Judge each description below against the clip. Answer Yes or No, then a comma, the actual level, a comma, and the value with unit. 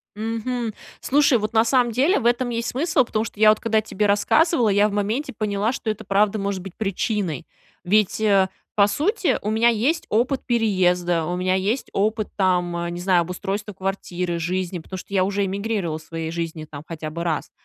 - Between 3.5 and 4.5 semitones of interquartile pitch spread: Yes, average, 3.8 semitones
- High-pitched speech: Yes, high, 205 Hz